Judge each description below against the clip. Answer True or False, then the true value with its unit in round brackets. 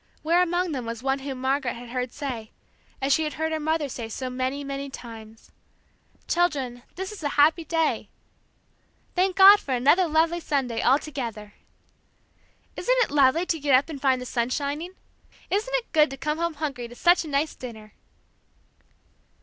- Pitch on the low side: False (280 Hz)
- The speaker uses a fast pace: False (180 wpm)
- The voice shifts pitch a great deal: False (4.3 semitones)